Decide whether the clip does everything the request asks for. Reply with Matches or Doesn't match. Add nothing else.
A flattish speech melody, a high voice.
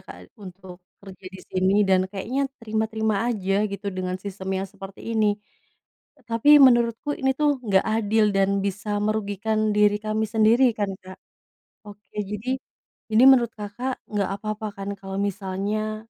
Matches